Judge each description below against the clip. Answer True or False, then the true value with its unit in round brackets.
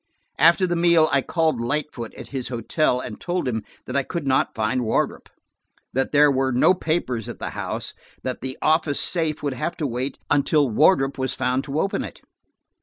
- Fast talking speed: False (195 wpm)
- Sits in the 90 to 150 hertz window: True (140 Hz)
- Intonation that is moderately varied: True (3.8 semitones)